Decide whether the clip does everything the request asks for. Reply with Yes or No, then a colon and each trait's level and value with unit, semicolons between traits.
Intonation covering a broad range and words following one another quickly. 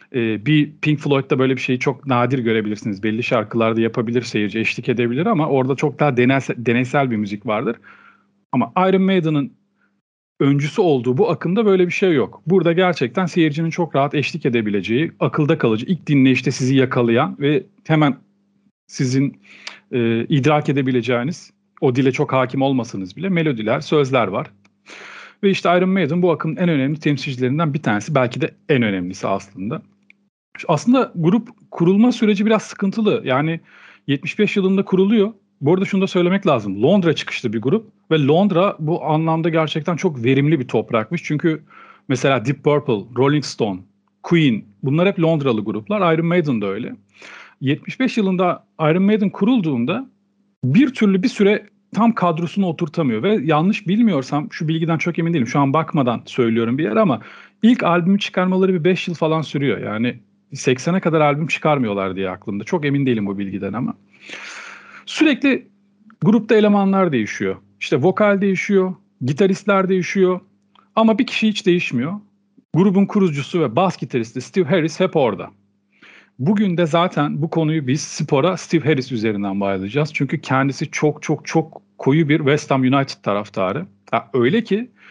Yes: wide, 6.3 semitones; fast, 155 wpm